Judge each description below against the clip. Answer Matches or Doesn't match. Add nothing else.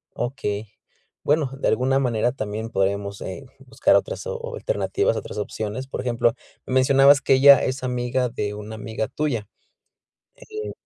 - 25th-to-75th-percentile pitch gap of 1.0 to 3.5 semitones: Doesn't match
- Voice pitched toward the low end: Matches